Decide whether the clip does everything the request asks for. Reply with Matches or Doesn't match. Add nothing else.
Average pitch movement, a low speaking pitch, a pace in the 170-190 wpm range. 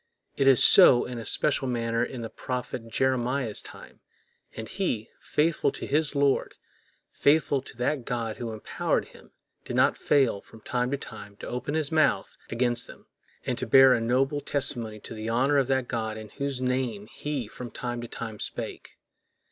Matches